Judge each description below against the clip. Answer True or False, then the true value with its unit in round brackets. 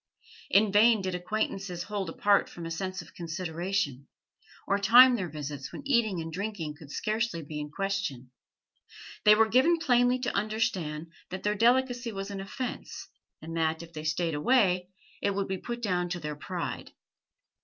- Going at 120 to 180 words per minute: True (170 wpm)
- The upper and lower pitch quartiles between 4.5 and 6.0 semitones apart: True (4.9 semitones)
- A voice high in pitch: True (195 Hz)